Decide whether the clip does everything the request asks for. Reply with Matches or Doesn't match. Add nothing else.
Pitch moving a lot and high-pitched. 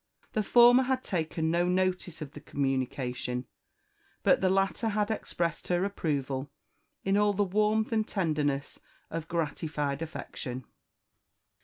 Doesn't match